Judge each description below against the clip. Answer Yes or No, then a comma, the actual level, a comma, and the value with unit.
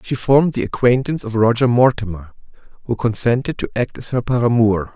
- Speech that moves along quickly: No, average, 170 wpm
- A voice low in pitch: Yes, low, 120 Hz